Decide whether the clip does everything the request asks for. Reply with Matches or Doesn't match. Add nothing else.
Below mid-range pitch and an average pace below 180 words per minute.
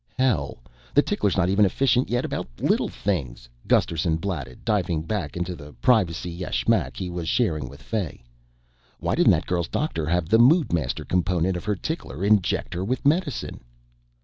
Matches